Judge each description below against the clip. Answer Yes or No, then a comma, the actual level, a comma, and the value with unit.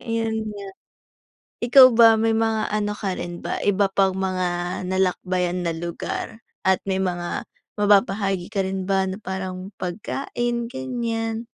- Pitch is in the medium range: No, high, 195 Hz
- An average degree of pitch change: Yes, average, 3.2 semitones